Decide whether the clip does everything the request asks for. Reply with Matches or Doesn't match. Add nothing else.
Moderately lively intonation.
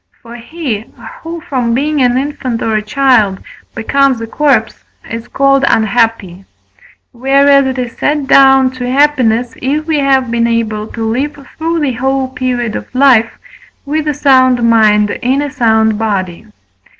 Matches